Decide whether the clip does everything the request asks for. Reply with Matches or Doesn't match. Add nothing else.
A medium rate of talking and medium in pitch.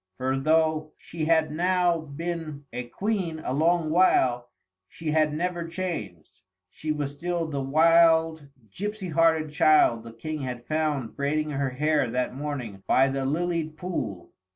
Matches